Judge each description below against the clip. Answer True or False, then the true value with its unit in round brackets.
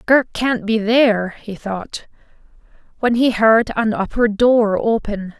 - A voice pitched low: False (220 Hz)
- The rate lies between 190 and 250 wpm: False (145 wpm)